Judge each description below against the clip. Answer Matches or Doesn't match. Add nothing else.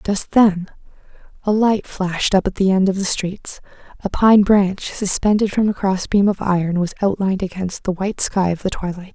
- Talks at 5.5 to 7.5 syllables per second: Doesn't match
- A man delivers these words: Doesn't match